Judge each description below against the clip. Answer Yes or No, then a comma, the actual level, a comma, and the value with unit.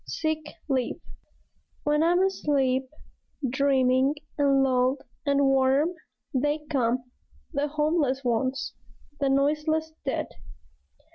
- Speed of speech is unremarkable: No, slow, 95 wpm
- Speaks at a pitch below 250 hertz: No, very high, 280 Hz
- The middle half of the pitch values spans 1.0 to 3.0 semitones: Yes, narrow, 2.5 semitones